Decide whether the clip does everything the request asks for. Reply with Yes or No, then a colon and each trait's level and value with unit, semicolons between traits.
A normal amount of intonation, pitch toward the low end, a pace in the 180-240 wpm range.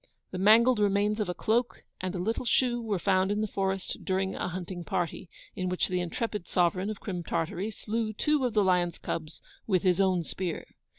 No: average, 3.1 semitones; high, 190 Hz; average, 200 wpm